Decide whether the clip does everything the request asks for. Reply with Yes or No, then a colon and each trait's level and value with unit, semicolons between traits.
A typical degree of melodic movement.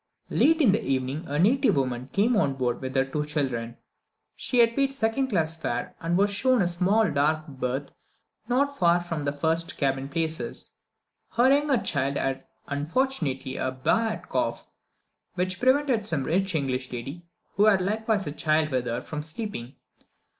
No: wide, 8.2 semitones